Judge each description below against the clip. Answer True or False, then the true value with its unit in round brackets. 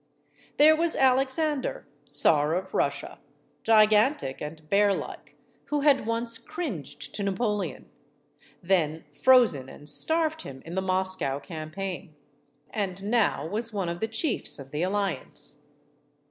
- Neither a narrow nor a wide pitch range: False (6.9 semitones)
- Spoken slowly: True (125 wpm)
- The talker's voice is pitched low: False (200 Hz)